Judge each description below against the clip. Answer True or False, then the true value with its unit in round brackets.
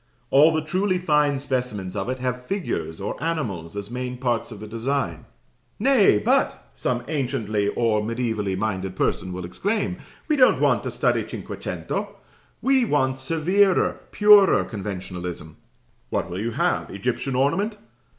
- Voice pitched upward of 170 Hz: False (125 Hz)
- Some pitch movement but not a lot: False (7.7 semitones)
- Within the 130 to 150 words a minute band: True (145 wpm)